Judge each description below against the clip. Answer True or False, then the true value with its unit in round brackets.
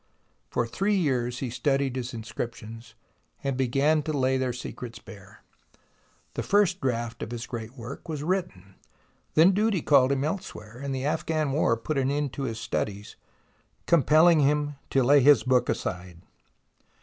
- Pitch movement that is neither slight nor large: True (4.1 semitones)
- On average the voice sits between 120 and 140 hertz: True (135 Hz)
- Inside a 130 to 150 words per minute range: False (160 wpm)